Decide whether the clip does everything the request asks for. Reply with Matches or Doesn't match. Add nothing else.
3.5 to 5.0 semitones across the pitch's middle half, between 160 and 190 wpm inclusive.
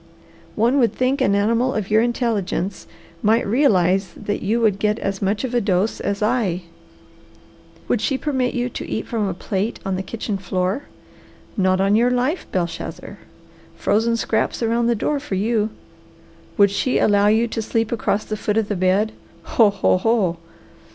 Doesn't match